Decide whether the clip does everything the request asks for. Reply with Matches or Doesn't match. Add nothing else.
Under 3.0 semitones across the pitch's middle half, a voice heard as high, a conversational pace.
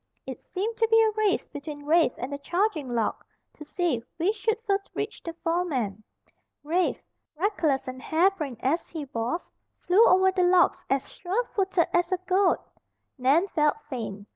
Doesn't match